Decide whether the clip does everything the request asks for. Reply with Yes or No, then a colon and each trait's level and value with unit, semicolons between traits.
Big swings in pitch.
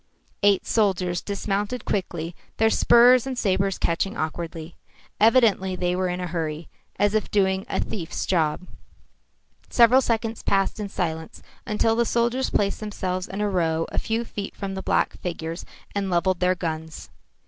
No: average, 3.7 semitones